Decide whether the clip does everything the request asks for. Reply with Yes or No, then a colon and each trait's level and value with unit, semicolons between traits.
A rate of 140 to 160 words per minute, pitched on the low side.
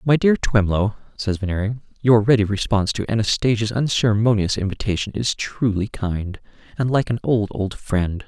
Yes: average, 150 wpm; low, 110 Hz